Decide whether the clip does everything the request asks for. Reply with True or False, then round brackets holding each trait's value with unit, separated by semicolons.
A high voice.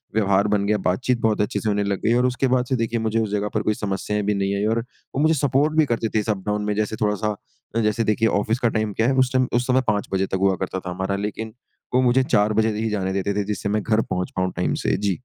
False (105 Hz)